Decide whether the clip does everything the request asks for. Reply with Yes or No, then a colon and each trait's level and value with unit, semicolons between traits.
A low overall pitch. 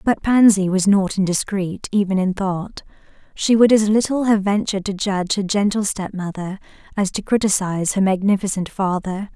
No: high, 195 Hz